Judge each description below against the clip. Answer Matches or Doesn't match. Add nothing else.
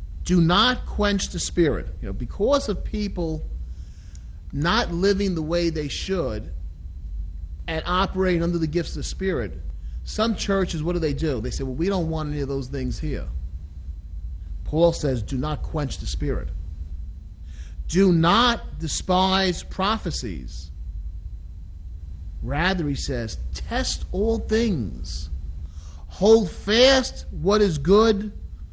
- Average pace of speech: Doesn't match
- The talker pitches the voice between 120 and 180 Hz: Matches